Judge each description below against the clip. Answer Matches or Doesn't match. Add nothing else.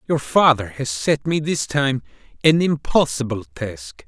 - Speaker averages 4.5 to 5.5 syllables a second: Doesn't match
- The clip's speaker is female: Doesn't match